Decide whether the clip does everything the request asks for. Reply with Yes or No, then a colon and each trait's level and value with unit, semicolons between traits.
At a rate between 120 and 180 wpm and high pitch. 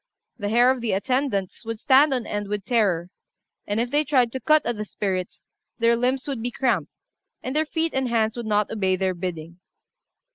No: fast, 205 wpm; high, 230 Hz